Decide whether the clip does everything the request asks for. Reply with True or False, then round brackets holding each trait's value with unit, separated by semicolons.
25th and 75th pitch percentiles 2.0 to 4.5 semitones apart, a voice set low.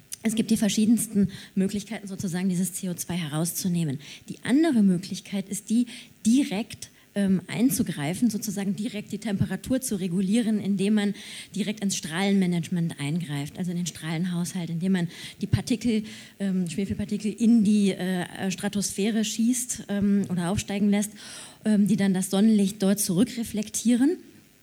False (2.8 semitones; 200 Hz)